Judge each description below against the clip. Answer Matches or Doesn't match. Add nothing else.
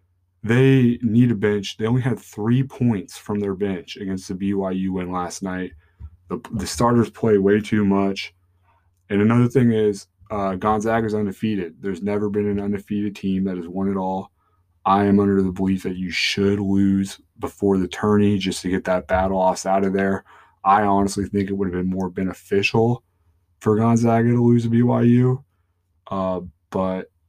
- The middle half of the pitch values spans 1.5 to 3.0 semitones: Matches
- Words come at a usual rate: Matches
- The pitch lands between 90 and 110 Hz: Matches